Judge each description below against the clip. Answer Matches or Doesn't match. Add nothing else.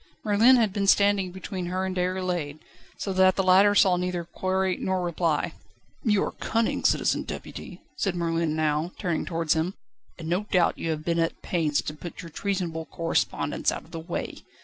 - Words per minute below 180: Doesn't match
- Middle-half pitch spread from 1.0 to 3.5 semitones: Matches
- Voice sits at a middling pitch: Matches